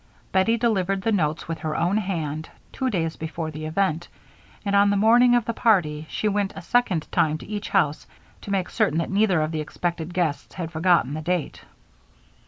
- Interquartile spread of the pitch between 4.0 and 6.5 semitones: Yes, average, 4.4 semitones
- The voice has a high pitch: No, medium, 180 Hz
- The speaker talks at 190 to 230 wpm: Yes, average, 195 wpm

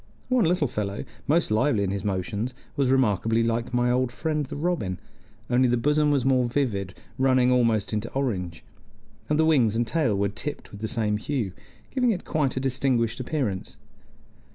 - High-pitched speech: No, low, 125 Hz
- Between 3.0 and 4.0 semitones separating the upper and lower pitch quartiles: No, average, 5.0 semitones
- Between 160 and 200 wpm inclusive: Yes, average, 175 wpm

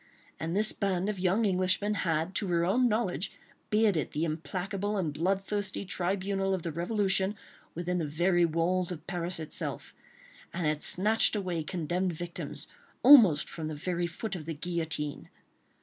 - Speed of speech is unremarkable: Yes, average, 155 wpm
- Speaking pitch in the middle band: Yes, medium, 180 Hz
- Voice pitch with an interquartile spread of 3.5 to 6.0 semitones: No, average, 3.0 semitones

